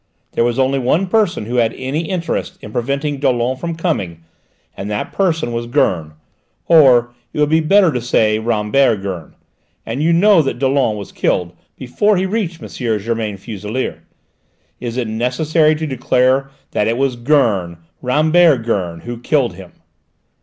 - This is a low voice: Yes, low, 125 Hz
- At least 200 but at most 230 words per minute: No, average, 160 wpm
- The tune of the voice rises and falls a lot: Yes, wide, 5.7 semitones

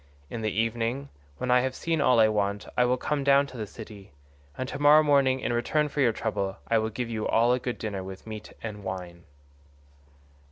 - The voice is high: No, low, 115 Hz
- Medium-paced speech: No, fast, 215 wpm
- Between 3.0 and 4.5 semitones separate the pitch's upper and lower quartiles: Yes, average, 3.6 semitones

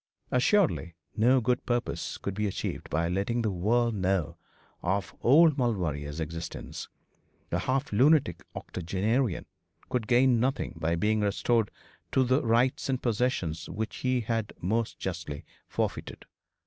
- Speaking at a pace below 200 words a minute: Yes, slow, 135 wpm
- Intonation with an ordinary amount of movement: No, wide, 5.8 semitones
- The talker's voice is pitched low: Yes, low, 110 Hz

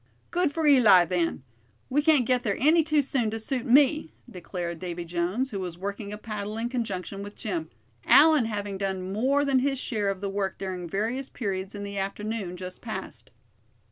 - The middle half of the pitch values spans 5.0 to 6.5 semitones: Yes, wide, 5.5 semitones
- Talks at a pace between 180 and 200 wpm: Yes, average, 190 wpm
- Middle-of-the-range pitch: No, high, 210 Hz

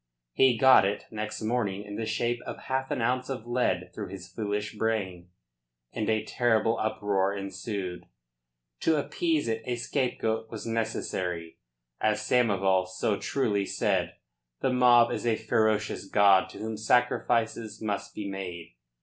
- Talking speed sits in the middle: Yes, average, 150 wpm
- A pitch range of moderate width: Yes, average, 3.0 semitones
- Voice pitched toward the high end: No, low, 110 Hz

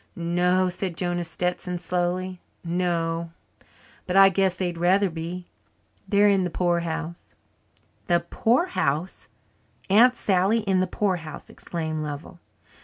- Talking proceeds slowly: Yes, slow, 115 wpm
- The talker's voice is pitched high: No, medium, 180 Hz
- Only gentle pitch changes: Yes, narrow, 1.9 semitones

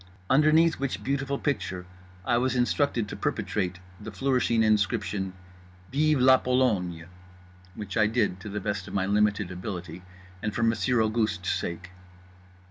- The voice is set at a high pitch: No, low, 110 Hz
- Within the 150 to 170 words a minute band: No, average, 140 wpm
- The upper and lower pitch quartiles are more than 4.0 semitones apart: Yes, average, 5.1 semitones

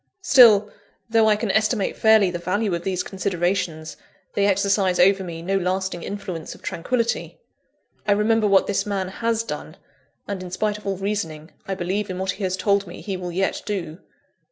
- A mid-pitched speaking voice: No, high, 195 Hz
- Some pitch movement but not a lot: No, narrow, 2.3 semitones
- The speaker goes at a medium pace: Yes, average, 185 wpm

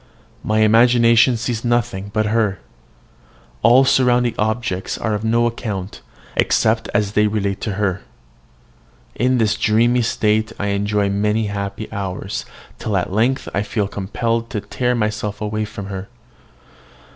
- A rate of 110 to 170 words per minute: Yes, average, 140 wpm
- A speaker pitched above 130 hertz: No, low, 110 Hz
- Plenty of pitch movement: No, narrow, 2.4 semitones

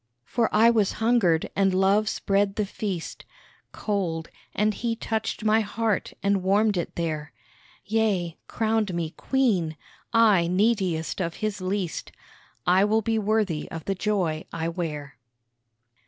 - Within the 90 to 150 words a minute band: Yes, average, 140 wpm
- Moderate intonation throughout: Yes, average, 4.1 semitones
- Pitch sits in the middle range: No, high, 200 Hz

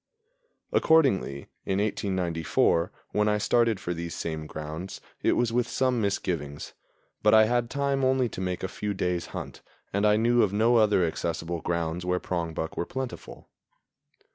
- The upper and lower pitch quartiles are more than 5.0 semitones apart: Yes, wide, 5.4 semitones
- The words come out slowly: No, average, 160 wpm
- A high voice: No, very low, 95 Hz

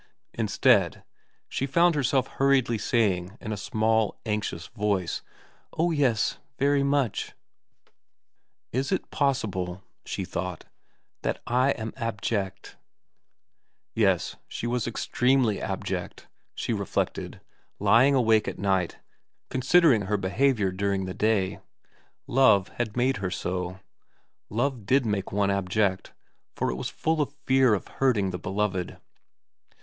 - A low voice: Yes, low, 110 Hz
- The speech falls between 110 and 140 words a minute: Yes, slow, 135 wpm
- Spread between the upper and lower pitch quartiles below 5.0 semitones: No, average, 5.3 semitones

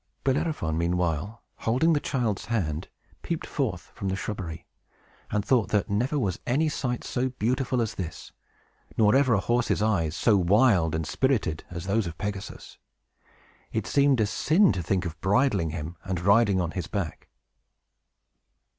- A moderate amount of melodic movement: No, wide, 6.0 semitones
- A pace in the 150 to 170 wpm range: Yes, average, 155 wpm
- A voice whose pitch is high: No, low, 105 Hz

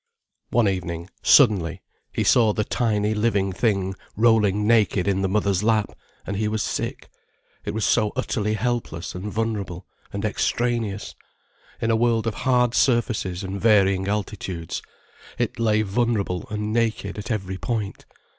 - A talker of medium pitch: No, low, 105 Hz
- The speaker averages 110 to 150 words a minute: Yes, average, 145 wpm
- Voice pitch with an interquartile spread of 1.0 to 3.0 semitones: Yes, narrow, 2.6 semitones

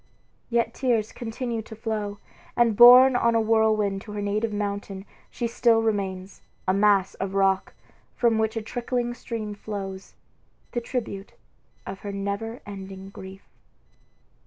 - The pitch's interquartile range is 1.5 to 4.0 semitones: Yes, average, 2.8 semitones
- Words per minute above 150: No, average, 140 wpm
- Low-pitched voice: No, high, 215 Hz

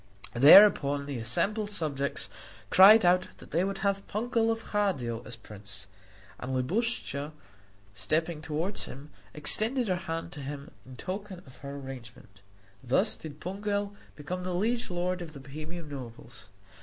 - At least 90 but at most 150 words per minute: Yes, average, 145 wpm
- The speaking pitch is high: No, medium, 165 Hz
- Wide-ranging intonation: Yes, wide, 6.4 semitones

